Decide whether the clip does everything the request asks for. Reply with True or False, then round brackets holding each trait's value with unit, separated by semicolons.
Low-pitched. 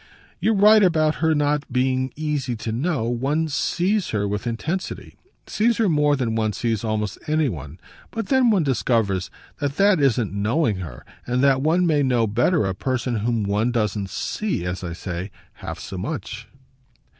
True (130 Hz)